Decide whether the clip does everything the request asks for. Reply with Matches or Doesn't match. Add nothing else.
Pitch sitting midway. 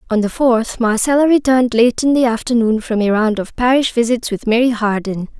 Doesn't match